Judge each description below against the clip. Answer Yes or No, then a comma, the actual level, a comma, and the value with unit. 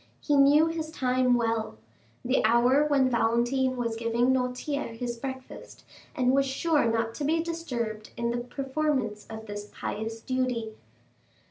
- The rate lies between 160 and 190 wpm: No, average, 140 wpm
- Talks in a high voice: Yes, very high, 250 Hz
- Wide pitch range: No, average, 3.2 semitones